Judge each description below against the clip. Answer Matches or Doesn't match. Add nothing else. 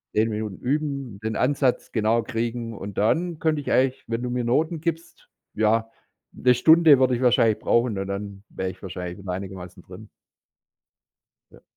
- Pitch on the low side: Matches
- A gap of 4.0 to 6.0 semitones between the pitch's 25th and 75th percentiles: Matches